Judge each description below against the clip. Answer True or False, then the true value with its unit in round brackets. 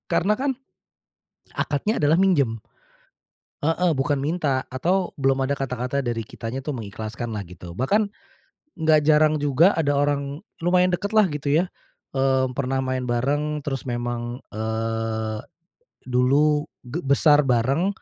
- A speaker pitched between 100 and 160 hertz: True (140 Hz)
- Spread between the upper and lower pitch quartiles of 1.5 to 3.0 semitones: False (4.0 semitones)